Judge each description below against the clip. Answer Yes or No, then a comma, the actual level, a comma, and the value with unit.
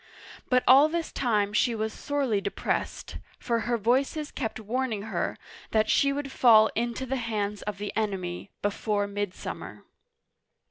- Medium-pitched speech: No, high, 225 Hz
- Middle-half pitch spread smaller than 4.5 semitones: Yes, average, 3.9 semitones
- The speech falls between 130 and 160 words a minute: Yes, average, 150 wpm